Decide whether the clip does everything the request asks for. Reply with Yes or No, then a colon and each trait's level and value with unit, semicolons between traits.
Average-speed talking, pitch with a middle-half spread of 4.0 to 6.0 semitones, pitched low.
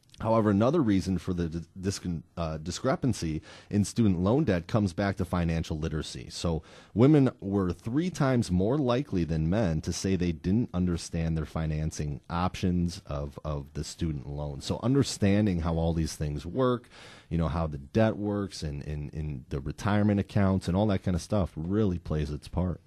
Yes: average, 180 wpm; average, 4.5 semitones; very low, 90 Hz